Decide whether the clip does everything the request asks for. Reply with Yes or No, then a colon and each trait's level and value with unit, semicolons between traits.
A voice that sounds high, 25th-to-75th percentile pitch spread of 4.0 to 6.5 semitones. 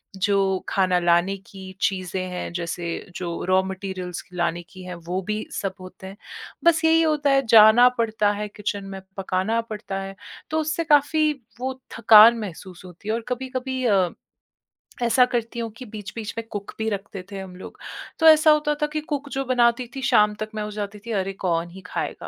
Yes: high, 210 Hz; average, 4.8 semitones